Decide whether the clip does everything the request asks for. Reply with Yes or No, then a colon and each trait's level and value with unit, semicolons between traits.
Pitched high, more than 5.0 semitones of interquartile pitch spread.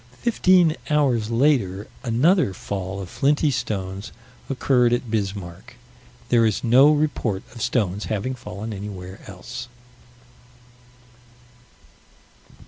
No: low, 115 Hz; wide, 5.4 semitones